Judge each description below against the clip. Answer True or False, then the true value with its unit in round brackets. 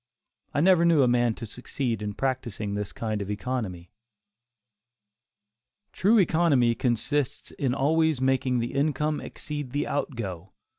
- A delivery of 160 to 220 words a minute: False (140 wpm)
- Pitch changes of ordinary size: True (4.4 semitones)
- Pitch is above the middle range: False (130 Hz)